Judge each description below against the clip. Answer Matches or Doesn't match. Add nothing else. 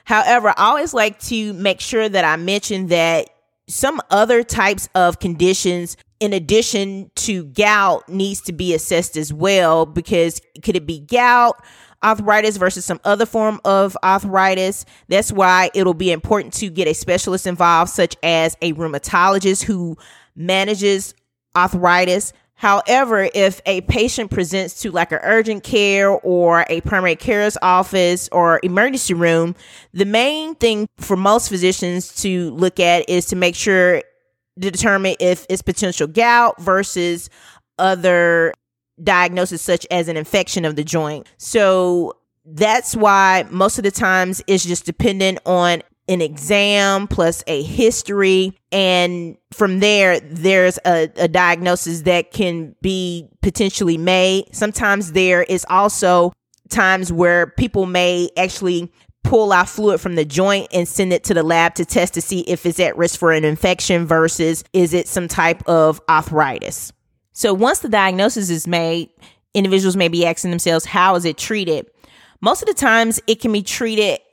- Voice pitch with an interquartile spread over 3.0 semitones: Doesn't match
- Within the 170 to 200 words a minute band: Doesn't match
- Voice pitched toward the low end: Doesn't match